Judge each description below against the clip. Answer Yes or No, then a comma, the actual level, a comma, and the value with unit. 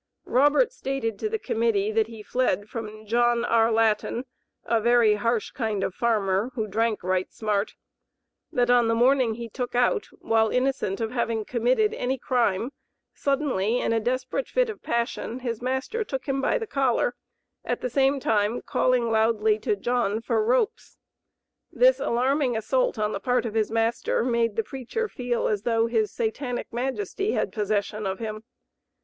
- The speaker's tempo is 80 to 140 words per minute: No, average, 170 wpm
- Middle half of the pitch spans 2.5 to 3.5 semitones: Yes, average, 2.8 semitones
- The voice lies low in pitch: No, high, 235 Hz